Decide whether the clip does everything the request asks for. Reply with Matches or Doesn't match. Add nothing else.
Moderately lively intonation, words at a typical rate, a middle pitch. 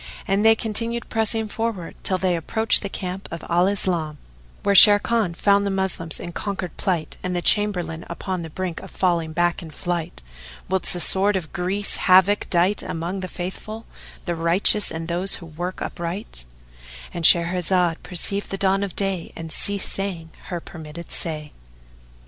Matches